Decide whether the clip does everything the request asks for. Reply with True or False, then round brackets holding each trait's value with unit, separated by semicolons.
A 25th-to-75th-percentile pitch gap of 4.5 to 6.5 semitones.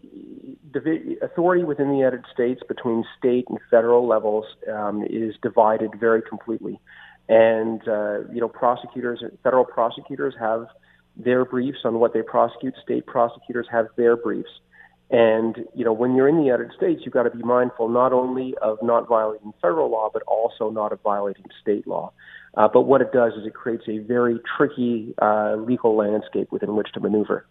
False (2.4 semitones)